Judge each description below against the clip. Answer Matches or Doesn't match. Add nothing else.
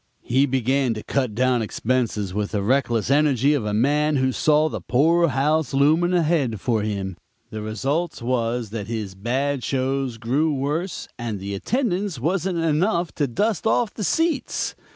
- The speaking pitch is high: Doesn't match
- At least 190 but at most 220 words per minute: Doesn't match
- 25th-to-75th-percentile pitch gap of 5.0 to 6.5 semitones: Matches